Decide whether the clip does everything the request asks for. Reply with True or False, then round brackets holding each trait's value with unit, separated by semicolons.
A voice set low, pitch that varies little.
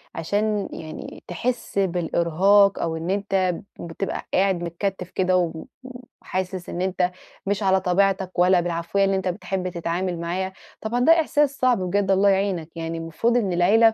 False (185 Hz; 2.3 semitones)